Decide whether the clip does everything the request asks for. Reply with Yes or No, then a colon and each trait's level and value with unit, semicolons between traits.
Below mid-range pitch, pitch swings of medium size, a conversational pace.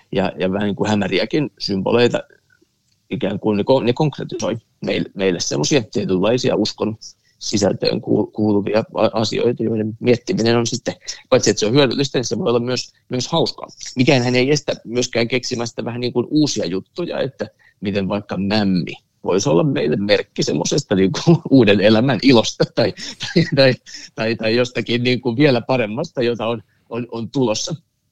No: low, 120 Hz; average, 3.0 semitones; fast, 165 wpm